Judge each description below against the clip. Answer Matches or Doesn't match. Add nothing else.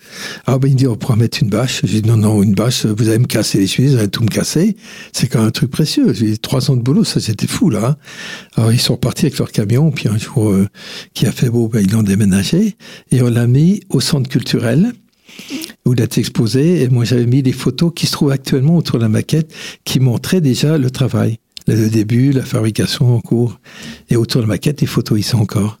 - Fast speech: Matches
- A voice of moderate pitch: Doesn't match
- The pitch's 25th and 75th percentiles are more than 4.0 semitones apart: Matches